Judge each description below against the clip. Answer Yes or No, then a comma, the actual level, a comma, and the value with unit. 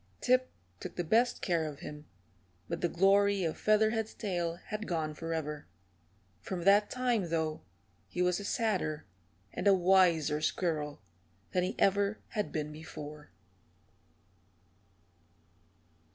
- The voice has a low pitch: No, medium, 180 Hz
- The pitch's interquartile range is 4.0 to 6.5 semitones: Yes, average, 4.4 semitones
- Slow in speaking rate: Yes, slow, 130 wpm